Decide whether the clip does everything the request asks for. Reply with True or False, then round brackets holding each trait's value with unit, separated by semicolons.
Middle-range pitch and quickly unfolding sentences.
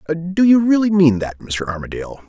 False (145 Hz; 185 wpm)